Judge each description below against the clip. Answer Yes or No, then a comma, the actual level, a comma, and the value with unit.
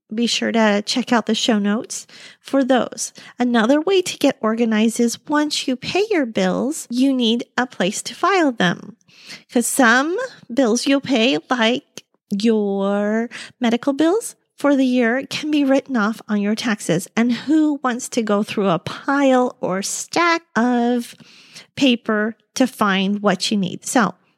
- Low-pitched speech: No, high, 240 Hz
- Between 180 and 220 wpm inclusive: No, average, 160 wpm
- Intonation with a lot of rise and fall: No, average, 4.1 semitones